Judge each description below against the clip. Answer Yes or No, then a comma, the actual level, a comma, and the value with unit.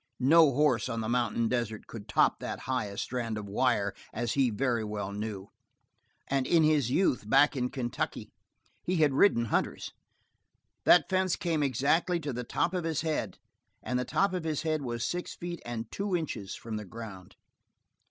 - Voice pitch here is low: Yes, low, 125 Hz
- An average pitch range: No, wide, 5.8 semitones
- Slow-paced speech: No, average, 180 wpm